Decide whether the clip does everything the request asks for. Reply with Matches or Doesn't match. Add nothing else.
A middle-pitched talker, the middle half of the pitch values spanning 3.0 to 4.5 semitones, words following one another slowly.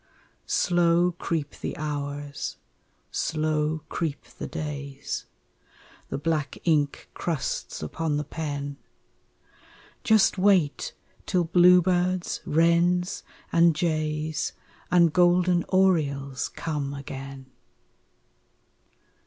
Matches